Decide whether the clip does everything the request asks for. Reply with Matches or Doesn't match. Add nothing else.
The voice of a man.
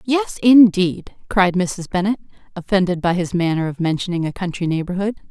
Doesn't match